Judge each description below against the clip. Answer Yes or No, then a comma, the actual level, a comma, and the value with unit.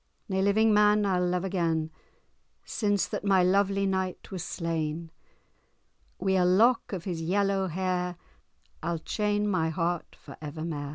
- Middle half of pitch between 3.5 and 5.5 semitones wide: No, average, 3.0 semitones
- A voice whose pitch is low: No, medium, 185 Hz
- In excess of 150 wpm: No, average, 145 wpm